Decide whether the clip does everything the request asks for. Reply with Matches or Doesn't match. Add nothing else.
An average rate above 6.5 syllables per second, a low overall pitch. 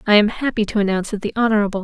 Doesn't match